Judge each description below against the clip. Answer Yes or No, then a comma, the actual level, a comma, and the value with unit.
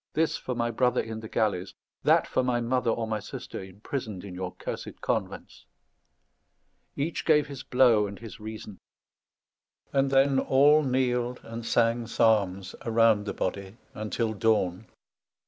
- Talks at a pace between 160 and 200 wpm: No, average, 150 wpm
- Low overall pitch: Yes, low, 115 Hz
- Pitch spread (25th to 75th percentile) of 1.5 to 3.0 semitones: No, average, 3.5 semitones